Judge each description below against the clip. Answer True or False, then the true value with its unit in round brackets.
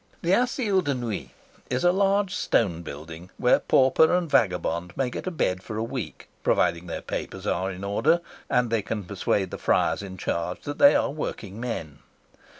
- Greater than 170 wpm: True (180 wpm)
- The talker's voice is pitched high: False (115 Hz)